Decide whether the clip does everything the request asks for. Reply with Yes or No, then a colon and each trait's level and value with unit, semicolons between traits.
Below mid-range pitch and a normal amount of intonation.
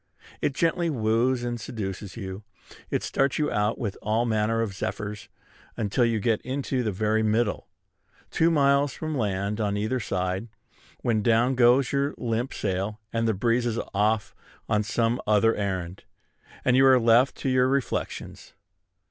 Yes: low, 115 Hz; average, 3.4 semitones